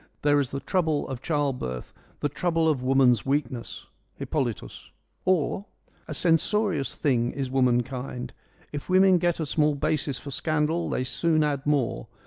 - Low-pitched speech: No, medium, 145 Hz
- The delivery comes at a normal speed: Yes, average, 165 wpm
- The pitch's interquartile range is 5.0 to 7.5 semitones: No, average, 3.9 semitones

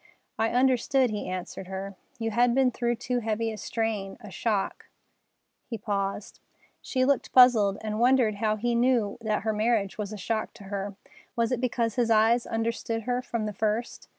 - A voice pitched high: Yes, high, 225 Hz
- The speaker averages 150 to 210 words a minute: Yes, average, 180 wpm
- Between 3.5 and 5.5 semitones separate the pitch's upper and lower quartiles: No, narrow, 2.5 semitones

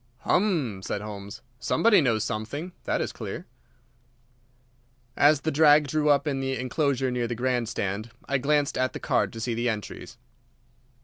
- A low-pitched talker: Yes, low, 130 Hz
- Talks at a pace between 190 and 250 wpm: No, average, 165 wpm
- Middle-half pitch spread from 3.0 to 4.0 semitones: No, average, 4.4 semitones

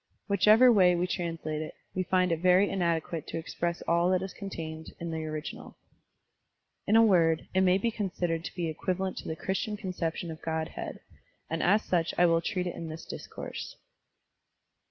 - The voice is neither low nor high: Yes, medium, 175 Hz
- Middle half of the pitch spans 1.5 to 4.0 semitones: Yes, narrow, 2.5 semitones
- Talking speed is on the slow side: No, average, 180 wpm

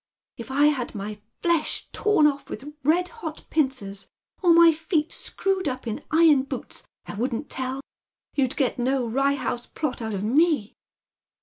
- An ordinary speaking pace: Yes, average, 170 wpm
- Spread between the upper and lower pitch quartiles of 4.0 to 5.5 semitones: Yes, average, 4.6 semitones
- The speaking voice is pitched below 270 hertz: No, very high, 275 Hz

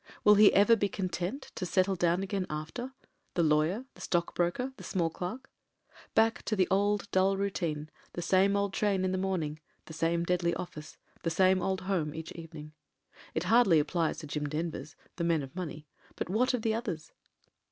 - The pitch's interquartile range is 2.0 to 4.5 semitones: Yes, average, 3.5 semitones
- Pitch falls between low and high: Yes, medium, 180 Hz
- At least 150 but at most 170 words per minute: No, fast, 205 wpm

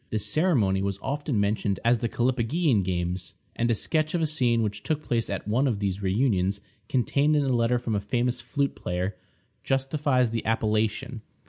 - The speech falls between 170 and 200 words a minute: Yes, average, 185 wpm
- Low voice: Yes, low, 115 Hz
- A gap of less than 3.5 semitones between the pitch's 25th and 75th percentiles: No, average, 4.7 semitones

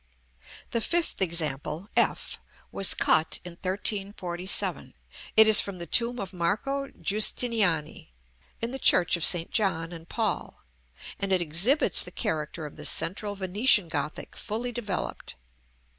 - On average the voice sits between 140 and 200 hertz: Yes, high, 190 Hz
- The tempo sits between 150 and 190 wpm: No, slow, 135 wpm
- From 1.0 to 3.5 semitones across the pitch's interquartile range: No, average, 4.4 semitones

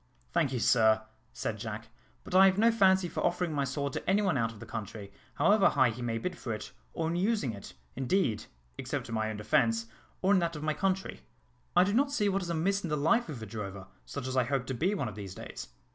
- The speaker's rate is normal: No, fast, 250 wpm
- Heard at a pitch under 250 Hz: Yes, medium, 140 Hz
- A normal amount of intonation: No, wide, 8.7 semitones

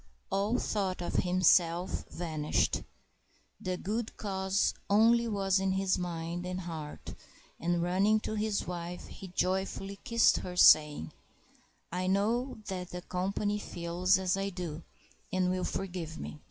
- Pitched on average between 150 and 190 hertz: Yes, medium, 185 Hz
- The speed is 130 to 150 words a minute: Yes, average, 140 wpm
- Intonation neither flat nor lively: No, narrow, 2.1 semitones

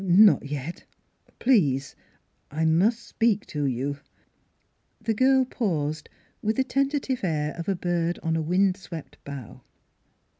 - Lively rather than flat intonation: Yes, wide, 6.7 semitones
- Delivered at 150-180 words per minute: No, slow, 135 wpm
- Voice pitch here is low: No, medium, 175 Hz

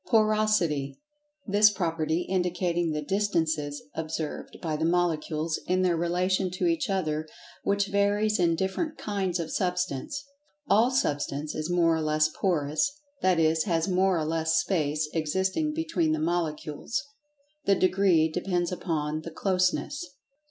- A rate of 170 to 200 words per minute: No, slow, 135 wpm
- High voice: No, medium, 175 Hz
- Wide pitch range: No, average, 4.0 semitones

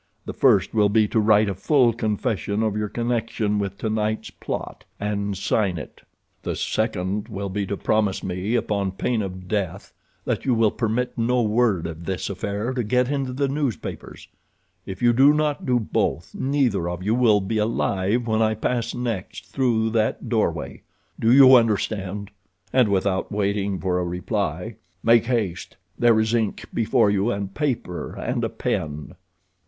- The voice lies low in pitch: Yes, low, 105 Hz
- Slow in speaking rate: No, average, 165 wpm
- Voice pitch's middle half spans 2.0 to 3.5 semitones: Yes, average, 3.2 semitones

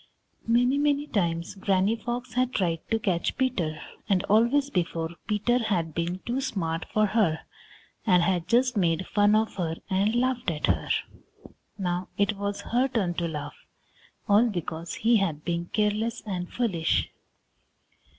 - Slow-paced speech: No, average, 150 wpm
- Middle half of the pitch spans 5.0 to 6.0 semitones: Yes, average, 5.3 semitones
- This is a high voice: Yes, high, 200 Hz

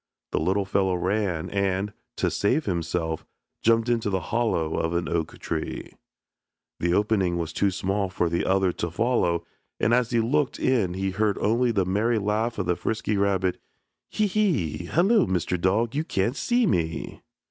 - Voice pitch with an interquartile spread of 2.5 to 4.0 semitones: No, average, 4.5 semitones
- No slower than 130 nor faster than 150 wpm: No, average, 170 wpm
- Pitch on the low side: Yes, low, 100 Hz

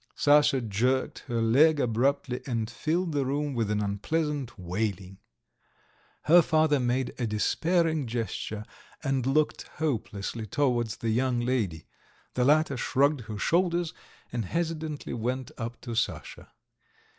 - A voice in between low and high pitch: No, low, 130 Hz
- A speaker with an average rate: No, slow, 130 wpm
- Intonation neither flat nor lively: Yes, average, 4.7 semitones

